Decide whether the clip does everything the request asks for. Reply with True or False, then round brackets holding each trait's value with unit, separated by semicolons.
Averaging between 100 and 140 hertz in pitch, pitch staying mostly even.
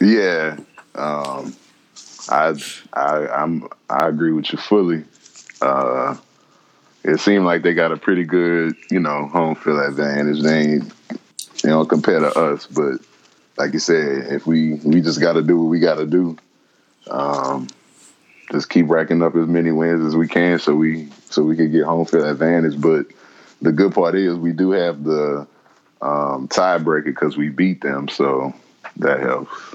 False (80 Hz; 2.3 semitones)